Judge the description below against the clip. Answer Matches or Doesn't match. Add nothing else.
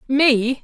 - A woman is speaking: Matches